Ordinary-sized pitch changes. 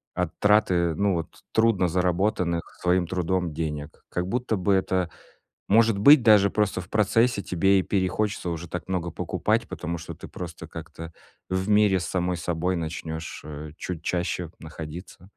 Yes: average, 3.0 semitones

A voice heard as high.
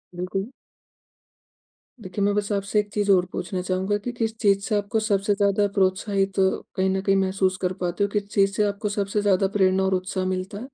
Yes: high, 195 Hz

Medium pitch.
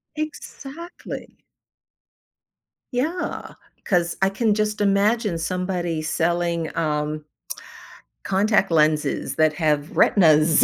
Yes: medium, 175 Hz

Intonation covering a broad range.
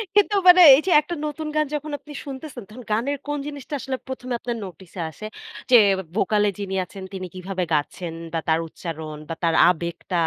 Yes: wide, 8.2 semitones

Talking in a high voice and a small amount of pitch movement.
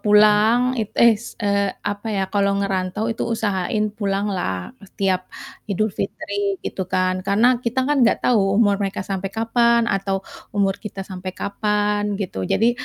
Yes: high, 205 Hz; narrow, 2.2 semitones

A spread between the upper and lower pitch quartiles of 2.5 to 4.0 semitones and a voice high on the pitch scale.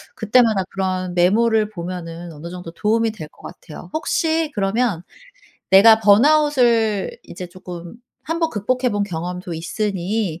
No: average, 4.4 semitones; high, 200 Hz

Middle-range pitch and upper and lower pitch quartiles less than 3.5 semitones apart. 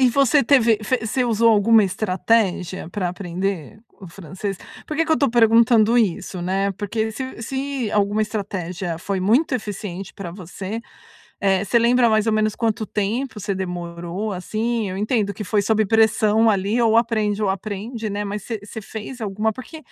No: high, 210 Hz; average, 2.9 semitones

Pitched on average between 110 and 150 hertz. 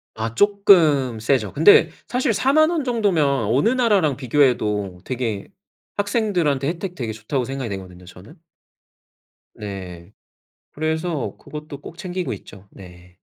Yes: medium, 140 Hz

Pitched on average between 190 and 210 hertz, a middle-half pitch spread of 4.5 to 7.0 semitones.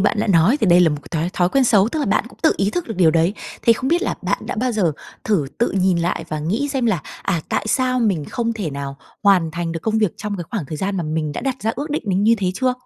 Yes: high, 200 Hz; wide, 5.6 semitones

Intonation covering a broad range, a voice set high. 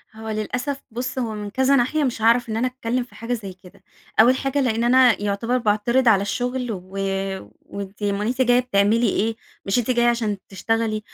No: average, 3.0 semitones; high, 230 Hz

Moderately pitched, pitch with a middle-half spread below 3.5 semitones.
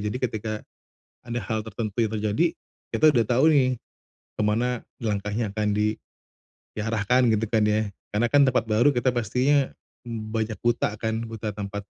No: low, 110 Hz; narrow, 2.4 semitones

